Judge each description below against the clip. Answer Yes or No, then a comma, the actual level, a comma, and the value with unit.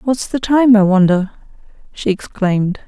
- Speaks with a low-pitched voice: No, high, 210 Hz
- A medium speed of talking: Yes, average, 145 wpm